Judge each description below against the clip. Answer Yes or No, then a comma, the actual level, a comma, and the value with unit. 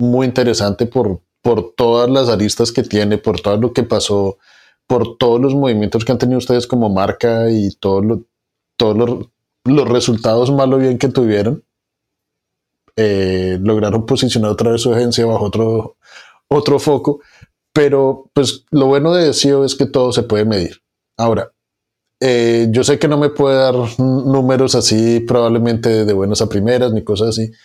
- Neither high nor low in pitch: No, low, 120 Hz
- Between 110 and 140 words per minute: No, average, 170 wpm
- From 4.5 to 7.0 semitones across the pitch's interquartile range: No, average, 3.2 semitones